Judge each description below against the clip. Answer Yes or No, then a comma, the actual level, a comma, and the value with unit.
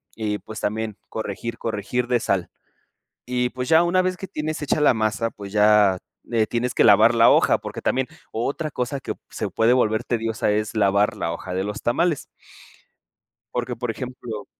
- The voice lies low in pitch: Yes, low, 115 Hz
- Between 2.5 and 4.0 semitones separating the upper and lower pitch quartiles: Yes, average, 3.1 semitones